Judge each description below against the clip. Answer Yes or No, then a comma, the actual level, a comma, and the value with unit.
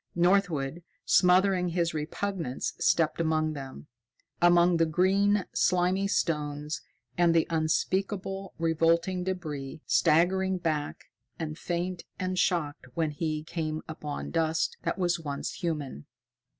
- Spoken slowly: Yes, slow, 115 wpm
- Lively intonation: No, average, 2.9 semitones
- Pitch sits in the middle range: Yes, medium, 170 Hz